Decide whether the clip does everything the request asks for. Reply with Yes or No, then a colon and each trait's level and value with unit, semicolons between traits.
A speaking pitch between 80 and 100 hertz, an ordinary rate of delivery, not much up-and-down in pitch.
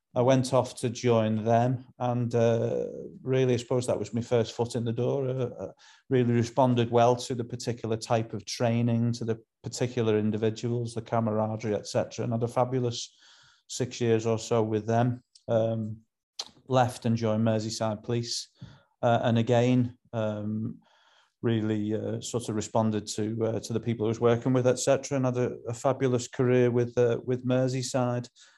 No: low, 120 Hz; average, 170 wpm; narrow, 1.8 semitones